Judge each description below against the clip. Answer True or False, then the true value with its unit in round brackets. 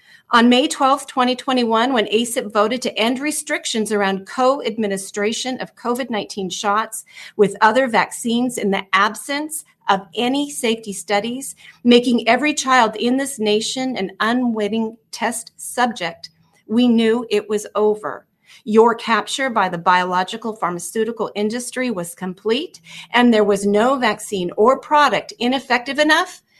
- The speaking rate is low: True (130 wpm)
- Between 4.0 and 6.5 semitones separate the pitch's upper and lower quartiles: False (3.4 semitones)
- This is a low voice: False (230 Hz)